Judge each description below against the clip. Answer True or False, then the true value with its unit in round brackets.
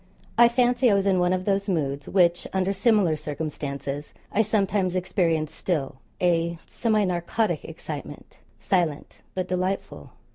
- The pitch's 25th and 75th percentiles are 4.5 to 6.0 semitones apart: False (3.4 semitones)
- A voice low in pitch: False (185 Hz)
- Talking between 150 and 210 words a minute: False (140 wpm)